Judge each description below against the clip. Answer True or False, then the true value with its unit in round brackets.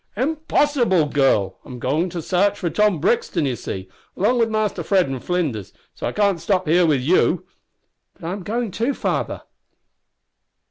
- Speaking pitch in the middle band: True (180 Hz)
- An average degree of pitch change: False (5.8 semitones)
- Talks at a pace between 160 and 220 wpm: True (170 wpm)